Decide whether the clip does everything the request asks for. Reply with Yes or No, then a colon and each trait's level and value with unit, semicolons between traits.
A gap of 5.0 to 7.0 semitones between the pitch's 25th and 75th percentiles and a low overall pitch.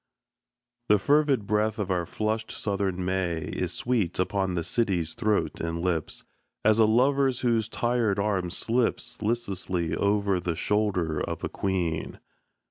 No: average, 3.9 semitones; low, 100 Hz